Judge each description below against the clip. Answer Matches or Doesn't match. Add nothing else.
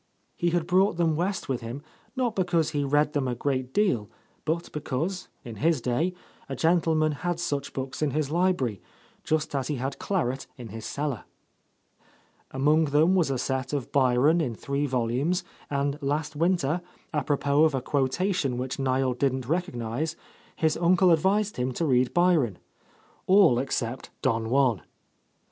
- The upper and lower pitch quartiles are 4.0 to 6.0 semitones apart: Matches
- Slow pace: Doesn't match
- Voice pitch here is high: Doesn't match